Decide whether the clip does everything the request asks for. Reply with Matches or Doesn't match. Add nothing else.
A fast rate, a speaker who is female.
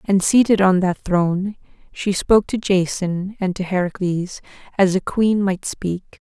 Doesn't match